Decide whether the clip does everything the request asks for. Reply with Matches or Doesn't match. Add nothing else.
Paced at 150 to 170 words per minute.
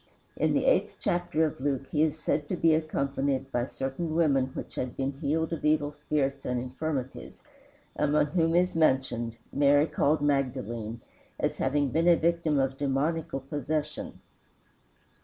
Matches